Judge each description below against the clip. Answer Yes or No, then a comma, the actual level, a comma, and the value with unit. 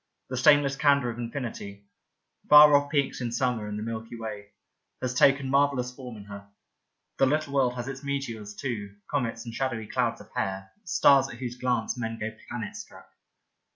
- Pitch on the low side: Yes, low, 125 Hz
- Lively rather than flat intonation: No, average, 3.6 semitones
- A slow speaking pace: No, average, 190 wpm